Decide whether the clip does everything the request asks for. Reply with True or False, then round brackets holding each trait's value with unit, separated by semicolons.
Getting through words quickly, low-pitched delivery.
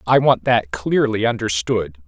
False (145 wpm; 105 Hz)